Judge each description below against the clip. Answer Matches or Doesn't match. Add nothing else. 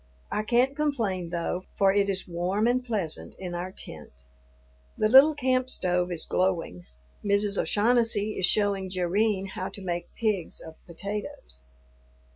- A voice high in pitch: Matches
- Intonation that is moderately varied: Matches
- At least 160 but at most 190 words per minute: Doesn't match